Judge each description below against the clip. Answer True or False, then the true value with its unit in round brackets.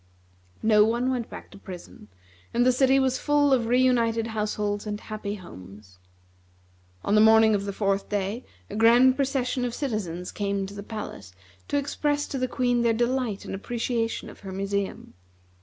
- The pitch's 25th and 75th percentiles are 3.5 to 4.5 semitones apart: True (3.9 semitones)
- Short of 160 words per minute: False (175 wpm)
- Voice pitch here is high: True (225 Hz)